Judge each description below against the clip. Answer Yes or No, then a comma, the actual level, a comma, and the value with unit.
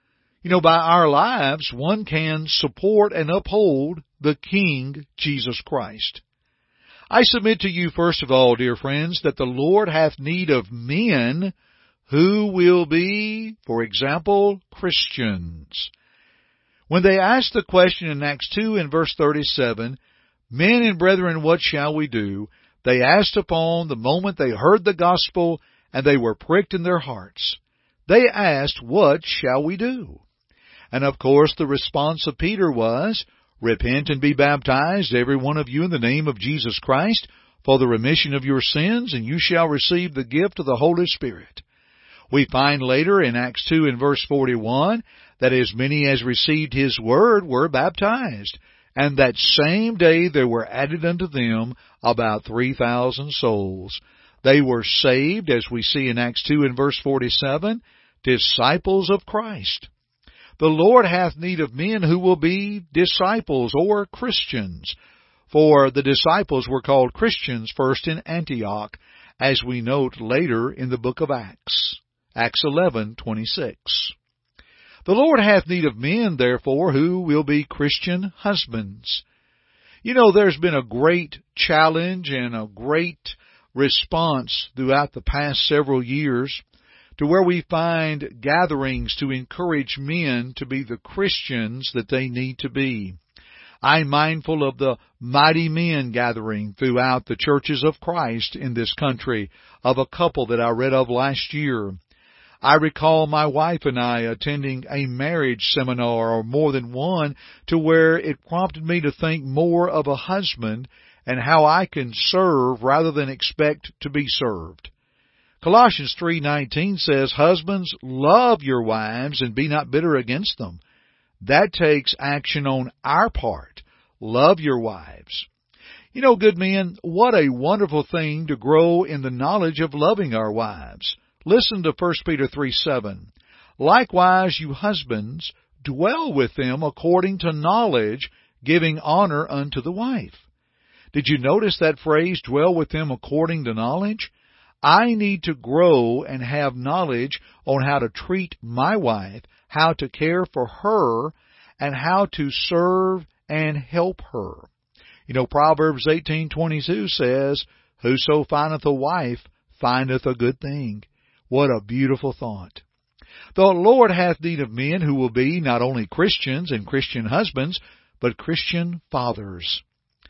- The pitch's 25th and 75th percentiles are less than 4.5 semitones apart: No, average, 5.1 semitones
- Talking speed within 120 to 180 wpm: Yes, average, 150 wpm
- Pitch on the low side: No, medium, 145 Hz